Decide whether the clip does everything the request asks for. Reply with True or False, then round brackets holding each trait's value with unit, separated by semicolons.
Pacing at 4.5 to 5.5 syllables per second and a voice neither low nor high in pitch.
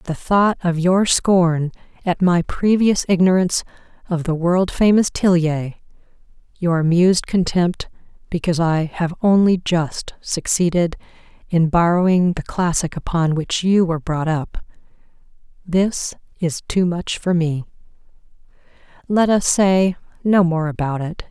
False (4.2 syllables/s; 175 Hz)